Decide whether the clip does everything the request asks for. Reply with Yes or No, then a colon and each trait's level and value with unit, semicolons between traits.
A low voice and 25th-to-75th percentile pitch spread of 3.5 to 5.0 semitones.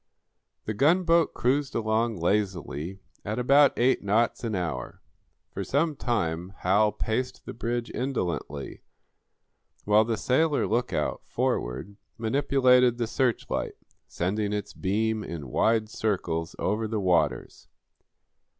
Yes: low, 110 Hz; average, 4.5 semitones